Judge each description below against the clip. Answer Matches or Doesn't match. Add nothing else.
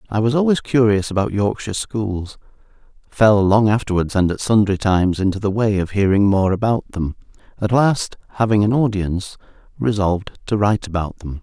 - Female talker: Doesn't match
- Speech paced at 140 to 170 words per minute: Matches